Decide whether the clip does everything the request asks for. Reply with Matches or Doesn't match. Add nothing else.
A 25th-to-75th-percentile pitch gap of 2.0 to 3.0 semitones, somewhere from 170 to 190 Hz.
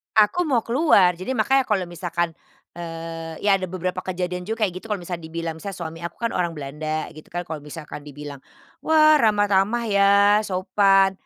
Doesn't match